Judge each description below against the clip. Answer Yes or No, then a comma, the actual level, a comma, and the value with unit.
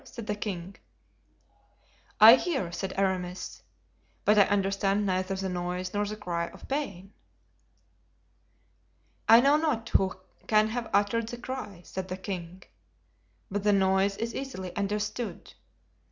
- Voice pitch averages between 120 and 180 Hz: No, high, 200 Hz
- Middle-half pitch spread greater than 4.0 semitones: No, average, 2.8 semitones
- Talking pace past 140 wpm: No, slow, 135 wpm